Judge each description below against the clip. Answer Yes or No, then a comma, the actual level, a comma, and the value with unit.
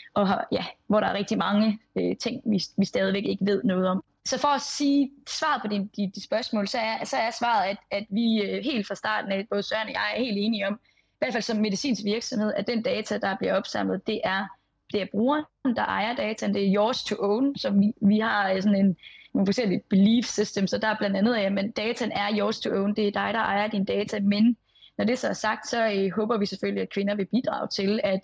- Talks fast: Yes, fast, 250 wpm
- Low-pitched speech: No, high, 210 Hz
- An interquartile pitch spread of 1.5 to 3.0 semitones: Yes, narrow, 2.5 semitones